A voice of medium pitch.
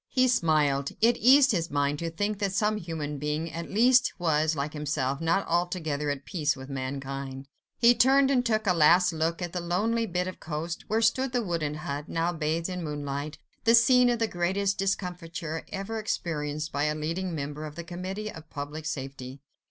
Yes: medium, 165 Hz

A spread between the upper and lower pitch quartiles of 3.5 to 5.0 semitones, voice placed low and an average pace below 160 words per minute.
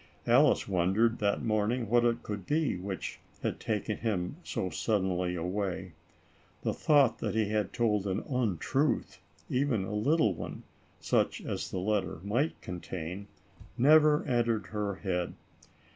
Yes: average, 4.0 semitones; low, 105 Hz; average, 140 wpm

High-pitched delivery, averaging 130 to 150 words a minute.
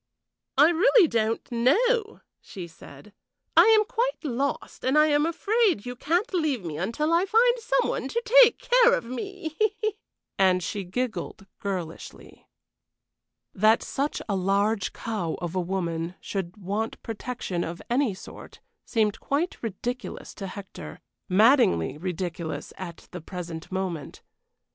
Yes: high, 225 Hz; average, 140 wpm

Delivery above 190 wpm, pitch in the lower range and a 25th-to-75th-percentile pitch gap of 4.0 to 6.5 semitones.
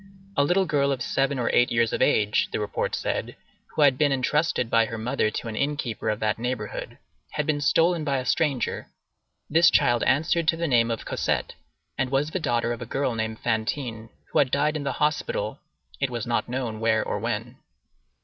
Yes: fast, 205 wpm; low, 130 Hz; average, 4.4 semitones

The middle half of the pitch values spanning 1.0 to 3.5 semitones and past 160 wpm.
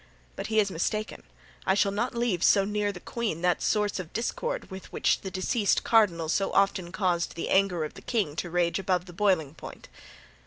Yes: average, 3.1 semitones; average, 200 wpm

